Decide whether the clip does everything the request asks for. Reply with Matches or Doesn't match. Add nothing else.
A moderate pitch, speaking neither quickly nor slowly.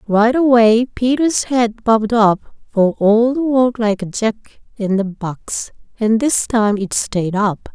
Doesn't match